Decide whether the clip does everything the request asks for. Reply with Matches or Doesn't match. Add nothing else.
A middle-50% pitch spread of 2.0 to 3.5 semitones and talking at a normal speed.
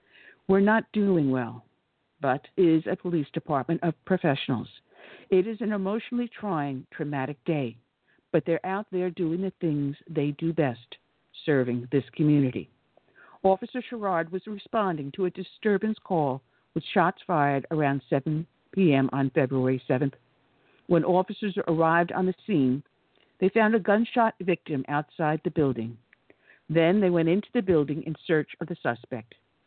Doesn't match